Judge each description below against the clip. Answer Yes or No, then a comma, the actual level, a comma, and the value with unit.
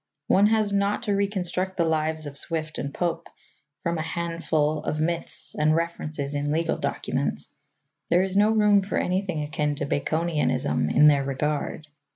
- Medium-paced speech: Yes, average, 165 wpm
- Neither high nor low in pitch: Yes, medium, 165 Hz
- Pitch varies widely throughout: No, average, 3.7 semitones